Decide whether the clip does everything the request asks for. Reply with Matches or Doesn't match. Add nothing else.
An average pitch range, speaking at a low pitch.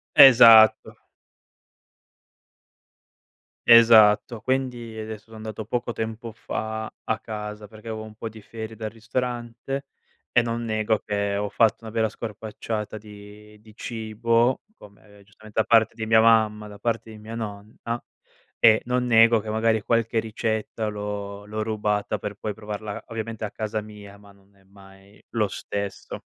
Doesn't match